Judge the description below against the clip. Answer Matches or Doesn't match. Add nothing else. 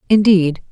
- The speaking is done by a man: Doesn't match